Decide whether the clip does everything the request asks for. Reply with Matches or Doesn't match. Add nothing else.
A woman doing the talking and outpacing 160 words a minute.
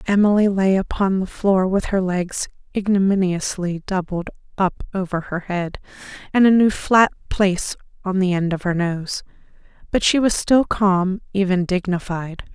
Doesn't match